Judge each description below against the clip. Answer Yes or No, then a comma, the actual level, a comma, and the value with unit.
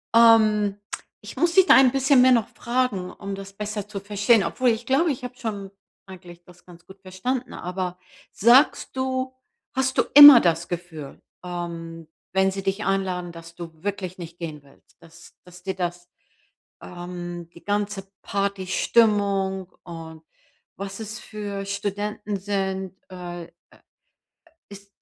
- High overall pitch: Yes, high, 195 Hz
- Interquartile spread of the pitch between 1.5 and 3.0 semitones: No, average, 3.4 semitones